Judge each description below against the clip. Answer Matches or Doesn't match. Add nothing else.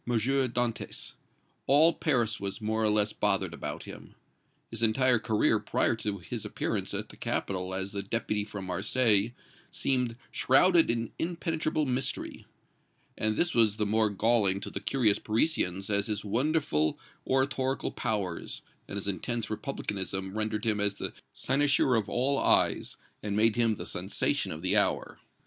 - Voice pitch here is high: Doesn't match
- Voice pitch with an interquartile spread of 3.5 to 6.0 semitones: Matches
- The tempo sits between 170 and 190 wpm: Doesn't match